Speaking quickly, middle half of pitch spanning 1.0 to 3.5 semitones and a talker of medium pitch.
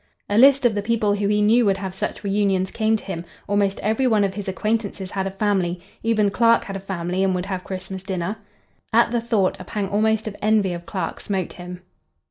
No: fast, 225 wpm; narrow, 2.4 semitones; high, 200 Hz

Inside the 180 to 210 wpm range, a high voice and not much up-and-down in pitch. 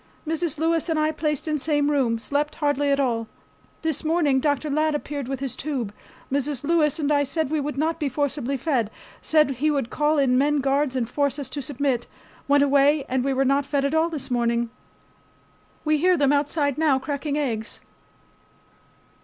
Yes: average, 190 wpm; very high, 285 Hz; narrow, 2.3 semitones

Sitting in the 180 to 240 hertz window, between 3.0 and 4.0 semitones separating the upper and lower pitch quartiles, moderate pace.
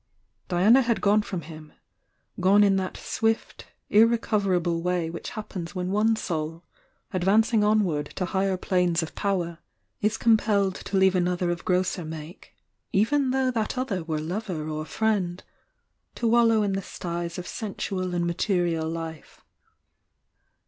Yes: medium, 185 Hz; average, 3.7 semitones; average, 150 wpm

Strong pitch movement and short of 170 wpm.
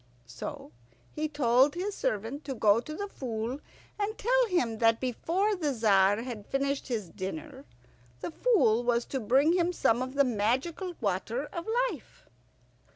Yes: wide, 6.3 semitones; average, 155 wpm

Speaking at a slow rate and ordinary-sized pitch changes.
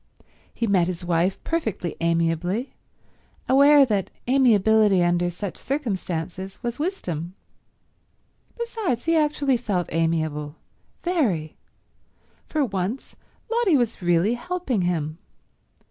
No: slow, 100 wpm; wide, 7.9 semitones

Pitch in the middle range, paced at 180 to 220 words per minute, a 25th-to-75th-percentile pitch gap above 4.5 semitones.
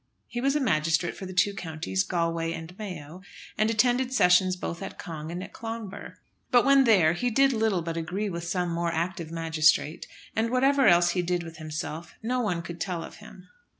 Yes: medium, 180 Hz; average, 200 wpm; average, 5.1 semitones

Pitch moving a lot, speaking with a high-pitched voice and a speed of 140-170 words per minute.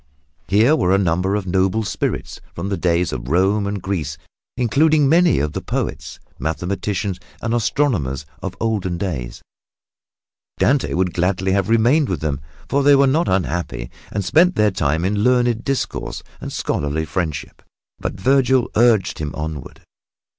No: wide, 5.9 semitones; low, 100 Hz; average, 155 wpm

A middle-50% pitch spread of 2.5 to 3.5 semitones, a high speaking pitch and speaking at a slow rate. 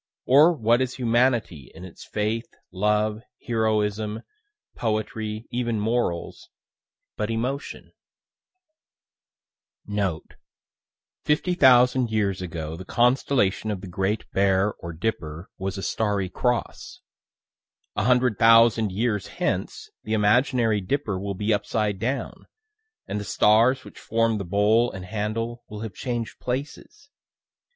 No: average, 3.1 semitones; low, 110 Hz; slow, 120 wpm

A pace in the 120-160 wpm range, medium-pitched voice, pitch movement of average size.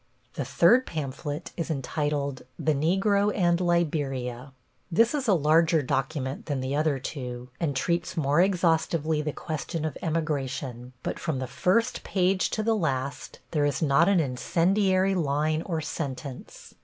Yes: average, 150 wpm; medium, 155 Hz; average, 4.0 semitones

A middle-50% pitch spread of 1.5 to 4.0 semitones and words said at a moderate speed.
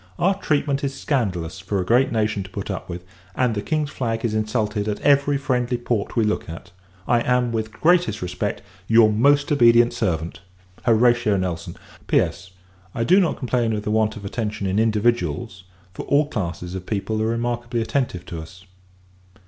Yes: average, 3.7 semitones; average, 180 wpm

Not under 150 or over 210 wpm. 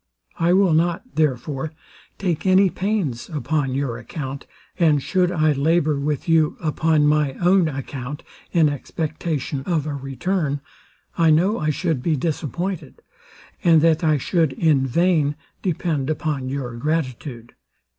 No: slow, 135 wpm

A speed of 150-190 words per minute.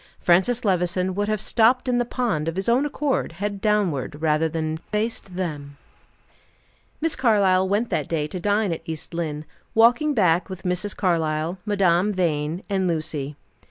Yes: average, 160 wpm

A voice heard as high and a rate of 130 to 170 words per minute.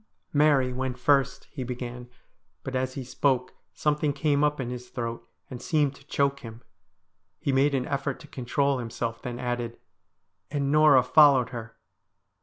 No: low, 130 Hz; average, 165 wpm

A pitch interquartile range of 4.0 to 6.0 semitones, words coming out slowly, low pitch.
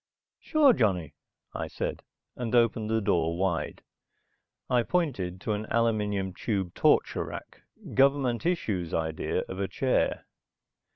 Yes: average, 5.0 semitones; slow, 125 wpm; low, 110 Hz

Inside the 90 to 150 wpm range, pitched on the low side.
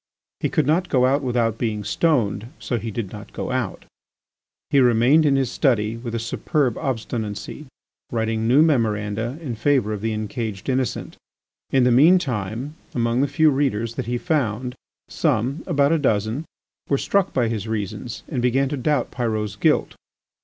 No: average, 170 wpm; low, 120 Hz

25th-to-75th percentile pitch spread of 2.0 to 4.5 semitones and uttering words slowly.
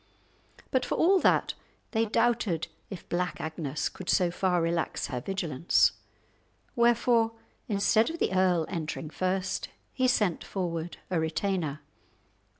No: average, 5.3 semitones; slow, 130 wpm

